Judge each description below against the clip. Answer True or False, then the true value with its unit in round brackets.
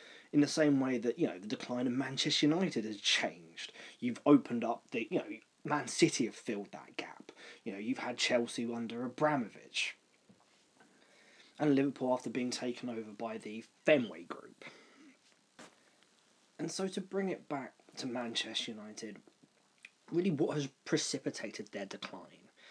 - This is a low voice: True (130 Hz)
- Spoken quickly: False (155 wpm)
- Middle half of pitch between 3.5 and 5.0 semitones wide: True (4.4 semitones)